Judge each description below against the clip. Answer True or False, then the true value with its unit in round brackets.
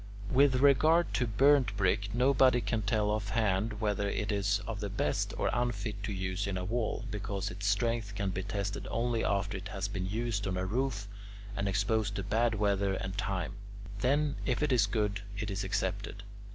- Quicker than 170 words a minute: True (190 wpm)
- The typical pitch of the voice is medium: False (105 Hz)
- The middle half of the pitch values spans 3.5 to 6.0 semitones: False (3.0 semitones)